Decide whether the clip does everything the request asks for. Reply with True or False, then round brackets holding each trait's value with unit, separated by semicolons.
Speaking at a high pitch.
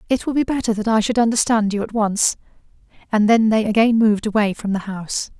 True (215 Hz)